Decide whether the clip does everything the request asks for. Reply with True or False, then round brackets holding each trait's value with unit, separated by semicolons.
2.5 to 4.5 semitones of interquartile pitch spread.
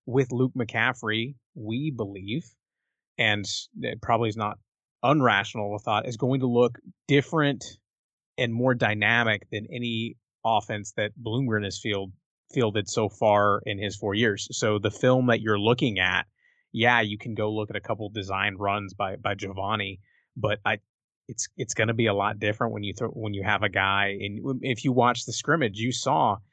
True (2.9 semitones)